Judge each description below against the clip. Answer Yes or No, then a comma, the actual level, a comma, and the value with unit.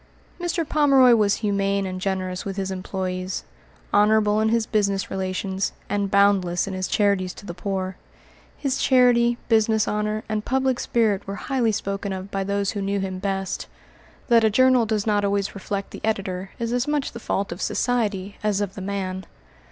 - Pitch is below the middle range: No, high, 200 Hz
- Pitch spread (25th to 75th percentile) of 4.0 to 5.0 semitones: No, narrow, 2.6 semitones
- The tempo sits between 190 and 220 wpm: No, average, 180 wpm